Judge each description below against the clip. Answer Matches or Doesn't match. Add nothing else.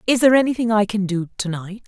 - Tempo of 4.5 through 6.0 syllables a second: Doesn't match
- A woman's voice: Matches